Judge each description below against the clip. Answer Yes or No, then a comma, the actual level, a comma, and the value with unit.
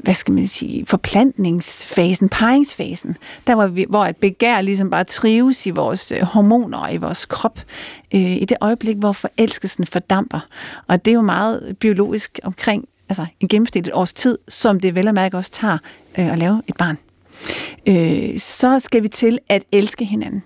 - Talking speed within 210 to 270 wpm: No, average, 175 wpm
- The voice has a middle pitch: No, high, 205 Hz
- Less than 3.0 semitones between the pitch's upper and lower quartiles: No, average, 3.4 semitones